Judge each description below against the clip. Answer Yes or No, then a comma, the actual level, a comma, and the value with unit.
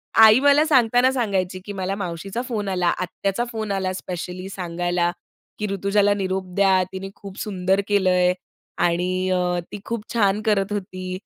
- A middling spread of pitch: No, narrow, 2.2 semitones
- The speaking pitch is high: Yes, high, 195 Hz